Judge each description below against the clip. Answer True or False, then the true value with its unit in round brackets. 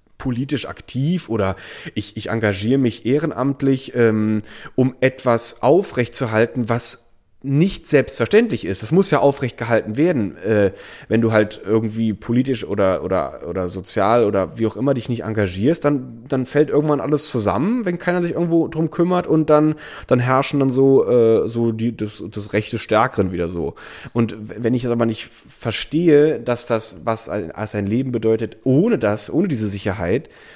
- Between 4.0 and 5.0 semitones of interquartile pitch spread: True (4.5 semitones)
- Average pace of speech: True (165 wpm)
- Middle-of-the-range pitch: False (120 Hz)